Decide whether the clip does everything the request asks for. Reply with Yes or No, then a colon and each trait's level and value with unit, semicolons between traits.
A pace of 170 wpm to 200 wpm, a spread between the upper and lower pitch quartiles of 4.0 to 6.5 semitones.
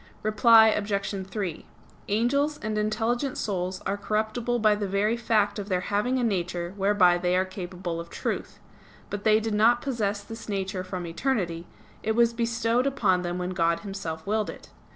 No: average, 175 wpm; average, 3.4 semitones